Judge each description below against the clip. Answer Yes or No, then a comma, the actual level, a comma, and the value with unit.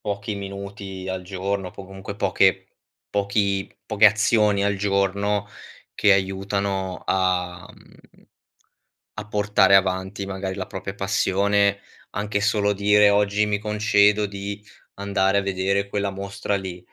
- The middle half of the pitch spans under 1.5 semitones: Yes, narrow, 1.1 semitones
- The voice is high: No, low, 100 Hz